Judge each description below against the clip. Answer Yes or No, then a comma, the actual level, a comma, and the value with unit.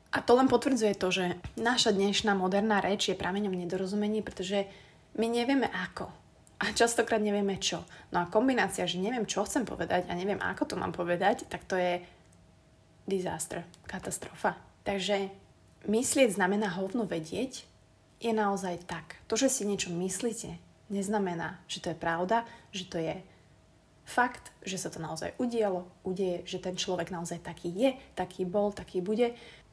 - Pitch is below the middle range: No, high, 200 Hz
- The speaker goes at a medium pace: Yes, average, 155 wpm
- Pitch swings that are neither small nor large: Yes, average, 3.6 semitones